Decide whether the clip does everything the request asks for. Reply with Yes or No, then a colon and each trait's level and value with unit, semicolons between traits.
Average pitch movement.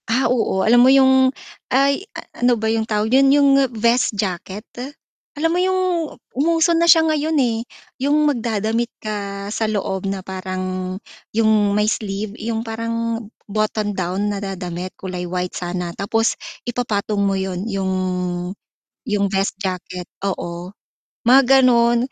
Yes: average, 4.2 semitones